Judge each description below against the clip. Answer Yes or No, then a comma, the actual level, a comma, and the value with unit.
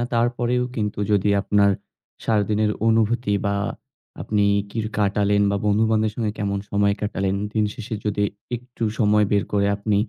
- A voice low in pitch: Yes, low, 105 Hz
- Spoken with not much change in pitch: Yes, narrow, 1.6 semitones